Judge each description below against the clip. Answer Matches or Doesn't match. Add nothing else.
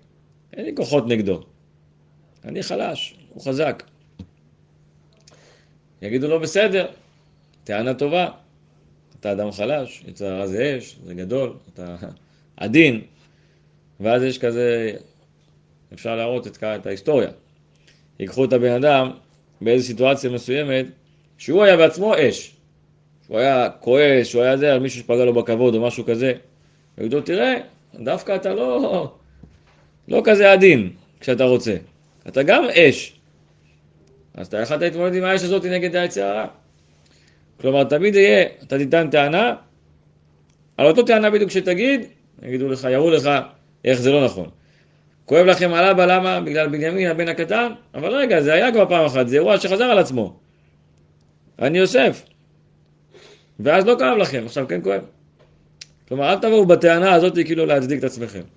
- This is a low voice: Matches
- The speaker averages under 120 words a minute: Doesn't match